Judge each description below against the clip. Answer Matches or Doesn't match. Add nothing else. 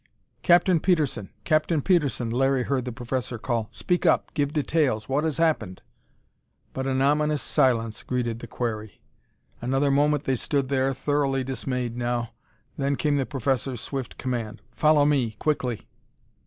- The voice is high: Doesn't match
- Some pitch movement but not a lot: Matches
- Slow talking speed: Doesn't match